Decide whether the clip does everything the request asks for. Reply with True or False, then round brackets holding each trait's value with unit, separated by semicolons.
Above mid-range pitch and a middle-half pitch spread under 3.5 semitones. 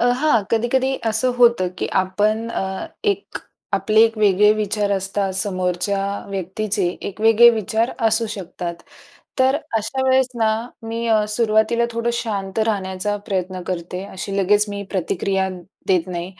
True (205 Hz; 2.9 semitones)